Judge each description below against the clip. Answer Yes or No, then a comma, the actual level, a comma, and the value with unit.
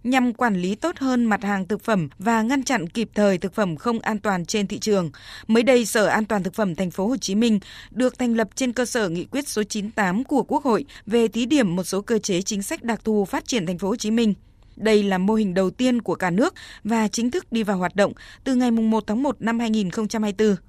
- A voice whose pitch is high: Yes, high, 220 Hz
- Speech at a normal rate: No, fast, 255 wpm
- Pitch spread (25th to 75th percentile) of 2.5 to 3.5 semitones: Yes, average, 3.2 semitones